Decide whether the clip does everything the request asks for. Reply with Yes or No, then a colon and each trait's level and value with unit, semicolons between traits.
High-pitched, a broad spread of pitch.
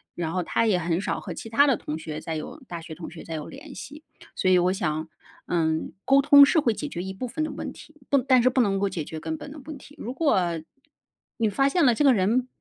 Yes: high, 210 Hz; wide, 8.4 semitones